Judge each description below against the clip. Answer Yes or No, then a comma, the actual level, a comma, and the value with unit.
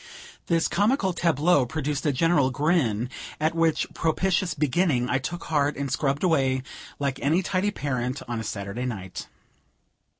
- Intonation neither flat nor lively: Yes, average, 4.6 semitones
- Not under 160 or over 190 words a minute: No, average, 145 wpm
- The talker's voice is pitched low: No, medium, 145 Hz